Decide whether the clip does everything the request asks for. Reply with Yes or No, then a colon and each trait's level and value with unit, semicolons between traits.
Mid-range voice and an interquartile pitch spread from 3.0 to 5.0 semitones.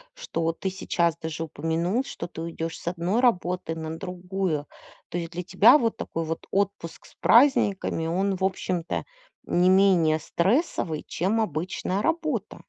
Yes: medium, 180 Hz; average, 3.3 semitones